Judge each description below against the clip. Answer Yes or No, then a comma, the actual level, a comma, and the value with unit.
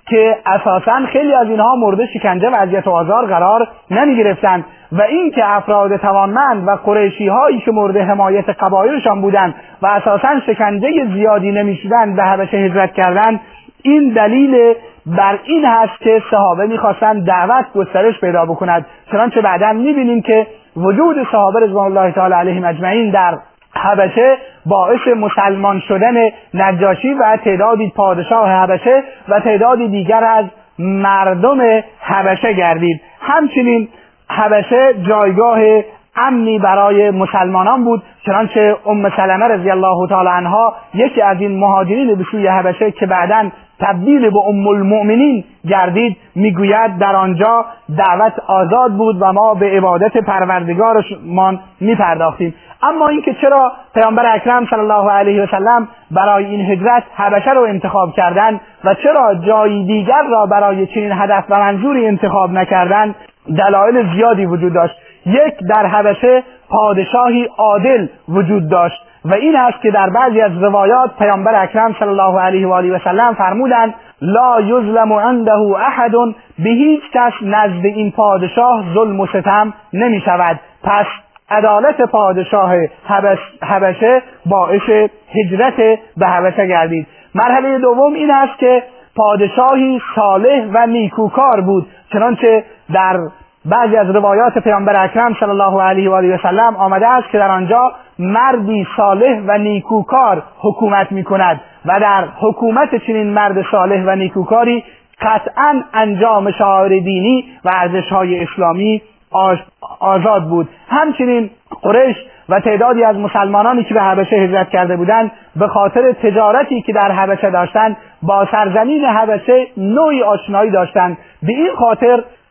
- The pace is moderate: Yes, average, 140 wpm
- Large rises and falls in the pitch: No, average, 3.1 semitones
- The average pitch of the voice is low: No, high, 210 Hz